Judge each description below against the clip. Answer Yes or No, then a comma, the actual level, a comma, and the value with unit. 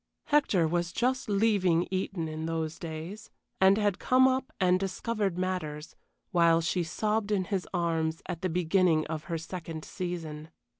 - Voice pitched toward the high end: No, medium, 180 Hz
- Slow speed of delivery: No, average, 155 wpm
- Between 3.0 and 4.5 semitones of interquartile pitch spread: Yes, average, 3.5 semitones